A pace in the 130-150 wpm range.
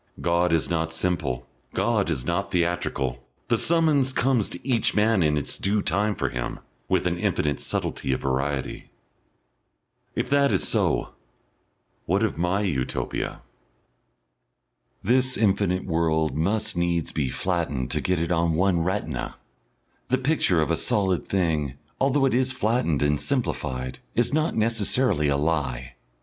Yes: average, 145 wpm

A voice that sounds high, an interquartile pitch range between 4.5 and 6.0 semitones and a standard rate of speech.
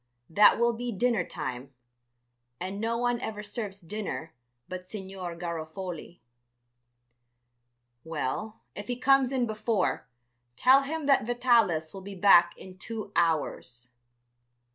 No: high, 200 Hz; wide, 5.4 semitones; slow, 120 wpm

